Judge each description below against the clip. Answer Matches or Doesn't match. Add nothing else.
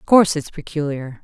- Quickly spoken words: Doesn't match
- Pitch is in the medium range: Matches